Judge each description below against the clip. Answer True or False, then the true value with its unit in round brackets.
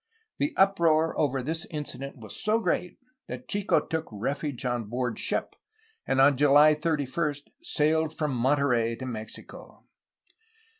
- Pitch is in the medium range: True (145 Hz)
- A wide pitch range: False (4.0 semitones)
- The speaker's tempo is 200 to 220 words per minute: False (135 wpm)